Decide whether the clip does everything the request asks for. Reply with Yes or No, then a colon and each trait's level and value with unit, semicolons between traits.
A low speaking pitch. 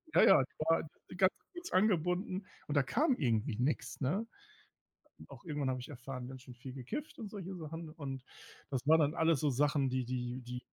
No: medium, 145 Hz